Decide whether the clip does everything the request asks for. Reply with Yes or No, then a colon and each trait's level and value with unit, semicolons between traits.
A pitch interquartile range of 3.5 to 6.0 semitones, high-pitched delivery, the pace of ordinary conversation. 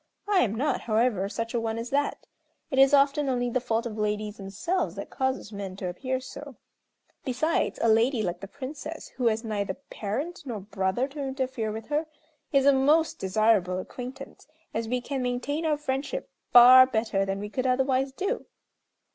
Yes: average, 4.2 semitones; very high, 250 Hz; average, 180 wpm